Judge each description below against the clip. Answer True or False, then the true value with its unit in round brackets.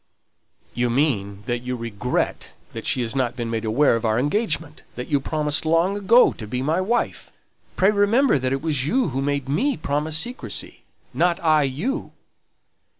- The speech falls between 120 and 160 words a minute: False (175 wpm)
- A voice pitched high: False (145 Hz)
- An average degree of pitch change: False (6.1 semitones)